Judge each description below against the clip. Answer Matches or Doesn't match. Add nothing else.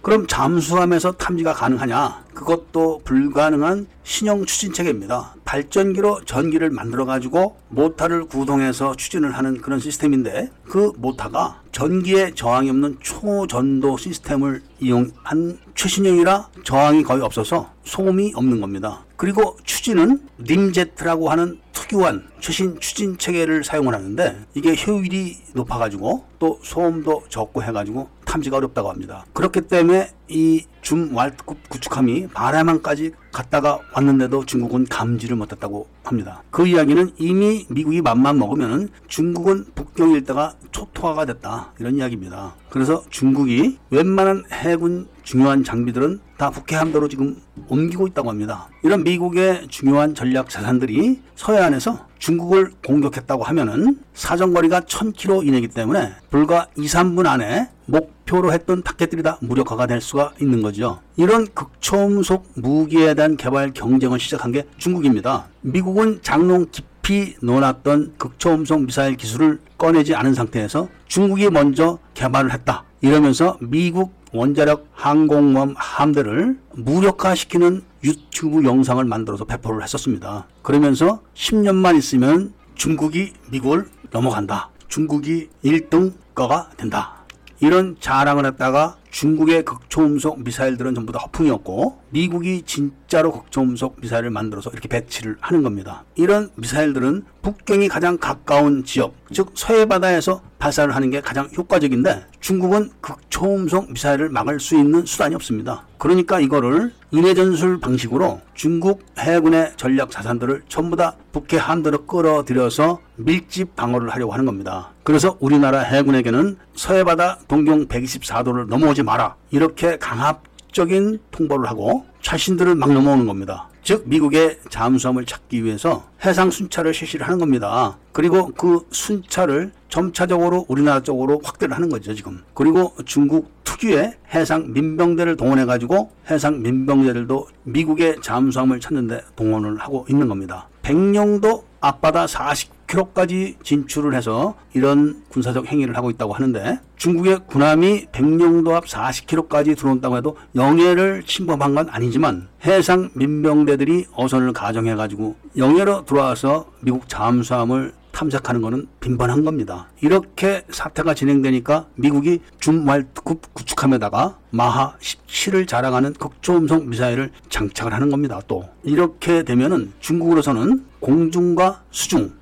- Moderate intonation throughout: Matches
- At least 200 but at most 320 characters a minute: Doesn't match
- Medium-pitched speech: Matches